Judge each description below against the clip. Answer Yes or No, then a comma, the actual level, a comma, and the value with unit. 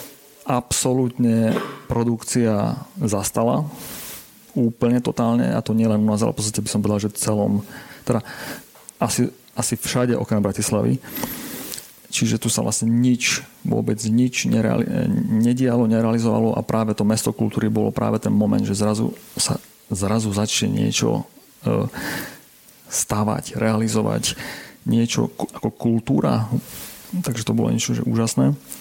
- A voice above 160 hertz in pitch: No, low, 115 Hz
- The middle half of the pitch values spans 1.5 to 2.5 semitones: Yes, narrow, 2.0 semitones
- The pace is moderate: Yes, average, 125 wpm